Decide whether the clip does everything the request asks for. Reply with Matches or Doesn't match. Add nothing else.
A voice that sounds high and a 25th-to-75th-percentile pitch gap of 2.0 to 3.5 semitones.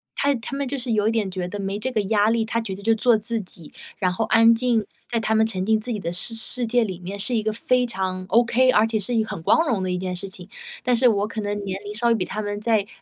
Matches